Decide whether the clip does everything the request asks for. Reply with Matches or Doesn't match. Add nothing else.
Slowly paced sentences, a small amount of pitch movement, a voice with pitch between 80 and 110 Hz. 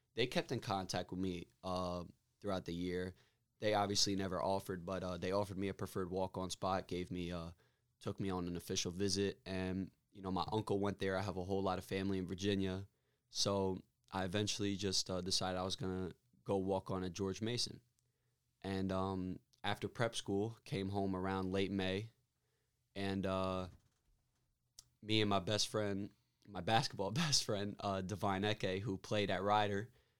Doesn't match